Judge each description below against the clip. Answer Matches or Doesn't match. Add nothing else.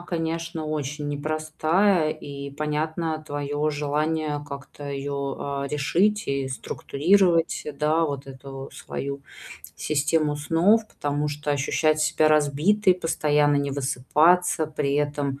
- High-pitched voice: Doesn't match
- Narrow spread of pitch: Matches